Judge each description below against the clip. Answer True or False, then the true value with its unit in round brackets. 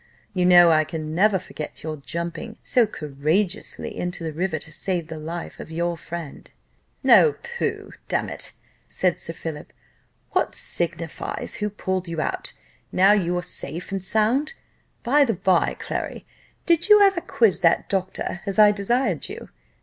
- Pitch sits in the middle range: True (180 Hz)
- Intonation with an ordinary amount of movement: True (4.1 semitones)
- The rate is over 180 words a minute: False (160 wpm)